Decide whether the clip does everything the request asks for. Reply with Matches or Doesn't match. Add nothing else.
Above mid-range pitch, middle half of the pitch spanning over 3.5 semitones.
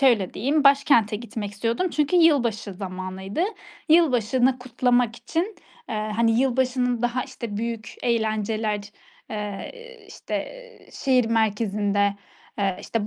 Matches